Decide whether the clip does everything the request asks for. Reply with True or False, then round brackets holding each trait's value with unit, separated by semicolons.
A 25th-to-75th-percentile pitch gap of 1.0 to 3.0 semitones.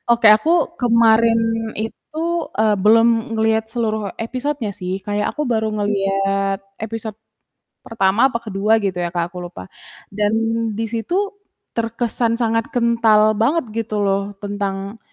True (2.4 semitones)